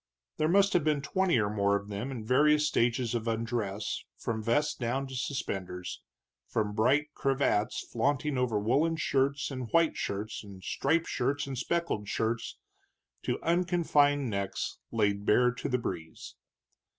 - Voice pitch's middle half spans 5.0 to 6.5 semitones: Yes, wide, 5.4 semitones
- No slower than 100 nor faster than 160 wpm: Yes, average, 150 wpm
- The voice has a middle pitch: No, low, 125 Hz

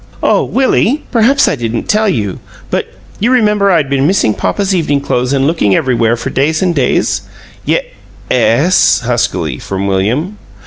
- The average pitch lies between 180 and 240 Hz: No, medium, 140 Hz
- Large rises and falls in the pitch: Yes, wide, 9.0 semitones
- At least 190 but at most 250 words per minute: No, average, 160 wpm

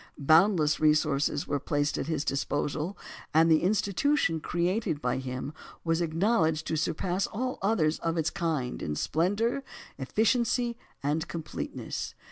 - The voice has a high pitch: No, medium, 160 Hz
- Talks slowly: Yes, slow, 130 wpm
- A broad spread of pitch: No, average, 4.8 semitones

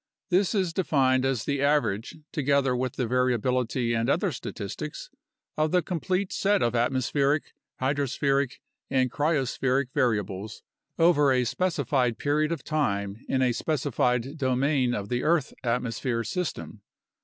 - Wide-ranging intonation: No, average, 3.7 semitones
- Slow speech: Yes, slow, 130 wpm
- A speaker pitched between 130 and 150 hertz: Yes, low, 135 Hz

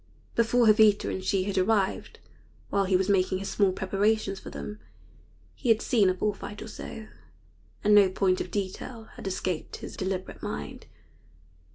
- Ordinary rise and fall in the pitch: No, narrow, 2.2 semitones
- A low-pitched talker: No, high, 195 Hz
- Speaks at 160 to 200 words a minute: Yes, average, 170 wpm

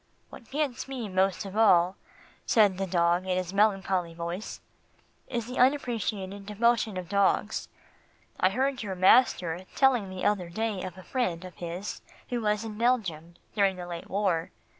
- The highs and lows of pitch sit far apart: No, average, 3.7 semitones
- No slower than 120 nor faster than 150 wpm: No, average, 160 wpm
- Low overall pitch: No, high, 195 Hz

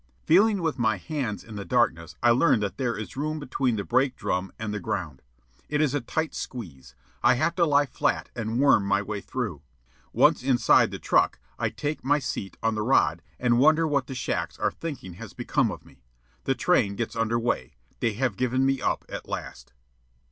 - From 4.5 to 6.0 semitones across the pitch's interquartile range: Yes, average, 5.3 semitones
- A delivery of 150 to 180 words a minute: No, fast, 205 wpm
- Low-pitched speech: Yes, low, 120 Hz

